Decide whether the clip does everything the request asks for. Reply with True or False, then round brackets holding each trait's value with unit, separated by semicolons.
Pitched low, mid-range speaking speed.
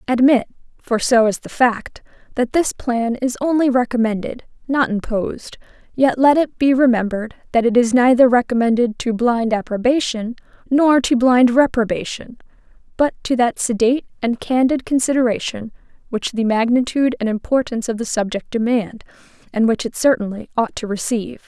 False (240 Hz; 150 wpm)